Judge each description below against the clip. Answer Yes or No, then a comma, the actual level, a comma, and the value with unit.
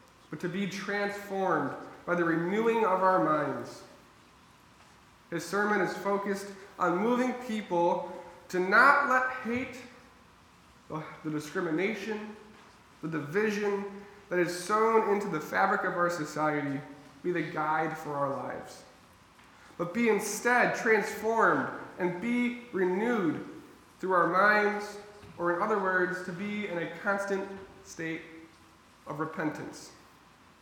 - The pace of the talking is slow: Yes, slow, 120 wpm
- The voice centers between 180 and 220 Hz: Yes, high, 190 Hz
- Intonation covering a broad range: No, average, 3.8 semitones